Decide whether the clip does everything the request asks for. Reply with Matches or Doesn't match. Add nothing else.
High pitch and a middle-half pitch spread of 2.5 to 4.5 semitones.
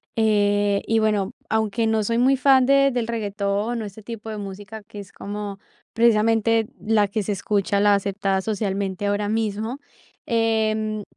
Doesn't match